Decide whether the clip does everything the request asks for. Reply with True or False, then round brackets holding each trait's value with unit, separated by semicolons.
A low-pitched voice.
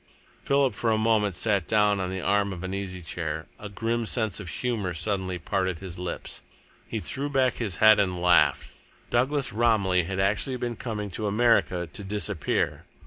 True (100 Hz)